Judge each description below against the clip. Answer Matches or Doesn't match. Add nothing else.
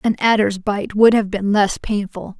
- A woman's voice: Matches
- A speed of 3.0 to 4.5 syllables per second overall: Matches